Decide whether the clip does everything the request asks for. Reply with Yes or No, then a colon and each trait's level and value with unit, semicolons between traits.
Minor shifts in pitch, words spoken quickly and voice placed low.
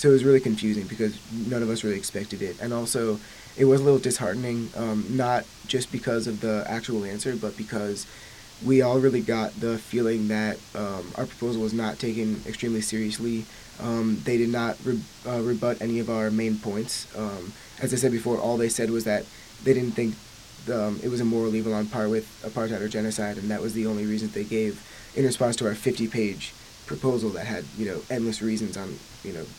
Yes: narrow, 1.9 semitones; fast, 215 wpm; low, 115 Hz